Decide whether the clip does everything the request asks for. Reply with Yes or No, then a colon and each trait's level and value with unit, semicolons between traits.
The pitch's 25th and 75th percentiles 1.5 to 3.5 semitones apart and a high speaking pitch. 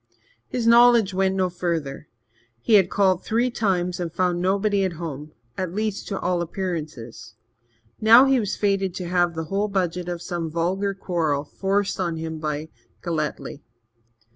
No: average, 3.1 semitones; medium, 180 Hz